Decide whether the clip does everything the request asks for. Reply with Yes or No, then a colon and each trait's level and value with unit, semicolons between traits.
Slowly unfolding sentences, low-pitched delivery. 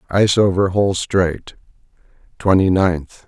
Yes: slow, 110 wpm; very low, 90 Hz